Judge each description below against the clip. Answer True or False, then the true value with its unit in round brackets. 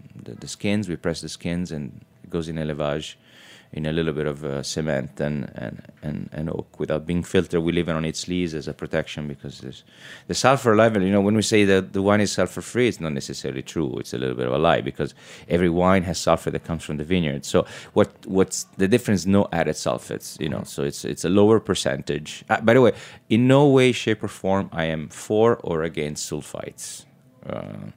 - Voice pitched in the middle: False (85 Hz)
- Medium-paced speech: False (225 wpm)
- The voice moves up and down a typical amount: True (4.9 semitones)